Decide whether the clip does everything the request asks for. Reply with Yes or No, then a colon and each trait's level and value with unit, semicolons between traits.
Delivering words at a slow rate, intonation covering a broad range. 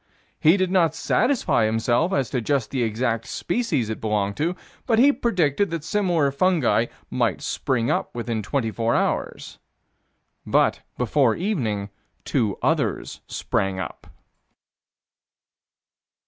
Yes: slow, 125 wpm; wide, 7.9 semitones